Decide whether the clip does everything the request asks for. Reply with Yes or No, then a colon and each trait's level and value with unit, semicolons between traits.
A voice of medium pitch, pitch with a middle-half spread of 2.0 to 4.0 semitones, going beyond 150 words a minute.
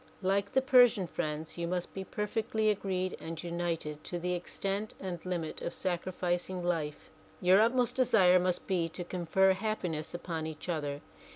Yes: medium, 180 Hz; narrow, 2.6 semitones; average, 165 wpm